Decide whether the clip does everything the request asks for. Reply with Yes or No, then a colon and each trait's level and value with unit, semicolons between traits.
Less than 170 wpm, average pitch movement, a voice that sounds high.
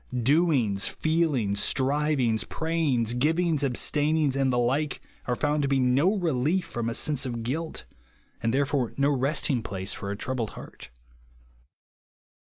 No: average, 140 wpm; average, 4.2 semitones; low, 135 Hz